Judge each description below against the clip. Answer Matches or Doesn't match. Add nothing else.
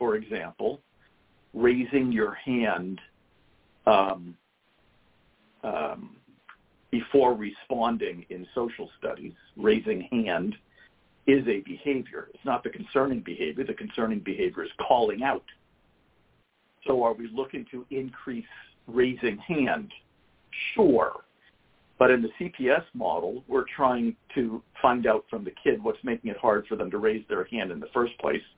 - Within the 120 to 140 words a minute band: Matches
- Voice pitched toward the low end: Matches